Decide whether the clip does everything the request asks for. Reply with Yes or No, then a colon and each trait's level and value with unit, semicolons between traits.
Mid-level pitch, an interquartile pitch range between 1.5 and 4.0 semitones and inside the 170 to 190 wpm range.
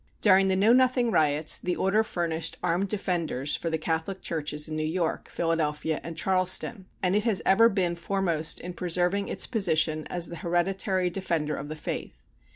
Yes: medium, 175 Hz; average, 3.2 semitones; average, 175 wpm